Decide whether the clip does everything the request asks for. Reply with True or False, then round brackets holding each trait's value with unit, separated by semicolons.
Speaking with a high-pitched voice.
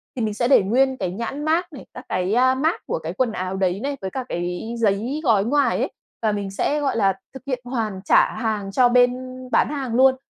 True (235 Hz)